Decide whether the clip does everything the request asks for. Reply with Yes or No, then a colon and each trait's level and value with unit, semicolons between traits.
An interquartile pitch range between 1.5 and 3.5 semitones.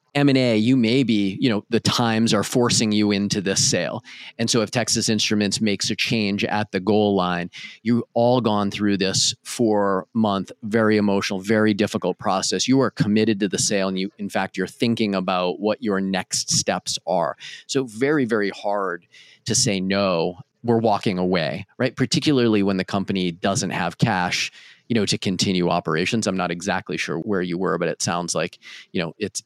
Yes: average, 2.9 semitones